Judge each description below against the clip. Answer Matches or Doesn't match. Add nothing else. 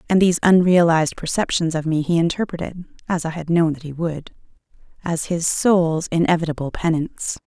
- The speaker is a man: Doesn't match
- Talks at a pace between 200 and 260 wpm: Doesn't match